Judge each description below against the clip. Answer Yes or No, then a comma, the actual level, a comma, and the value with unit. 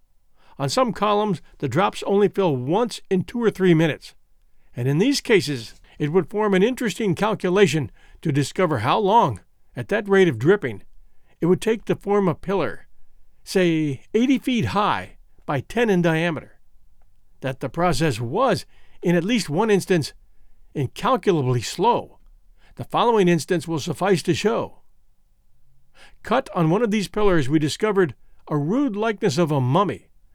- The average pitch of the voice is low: No, medium, 175 Hz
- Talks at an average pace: Yes, average, 155 wpm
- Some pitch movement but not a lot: No, wide, 7.0 semitones